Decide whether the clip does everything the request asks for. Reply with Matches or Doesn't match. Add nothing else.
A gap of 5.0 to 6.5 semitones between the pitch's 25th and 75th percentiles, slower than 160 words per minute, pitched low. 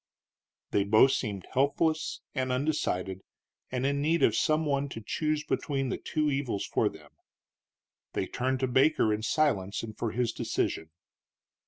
Matches